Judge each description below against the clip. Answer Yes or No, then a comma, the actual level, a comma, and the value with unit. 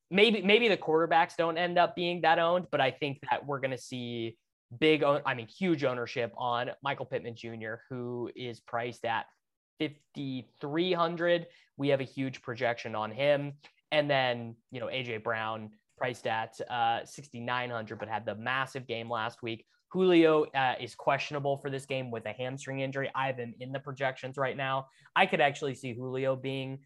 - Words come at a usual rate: Yes, average, 190 wpm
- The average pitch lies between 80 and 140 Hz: Yes, low, 135 Hz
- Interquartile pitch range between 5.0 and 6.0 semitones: No, average, 3.8 semitones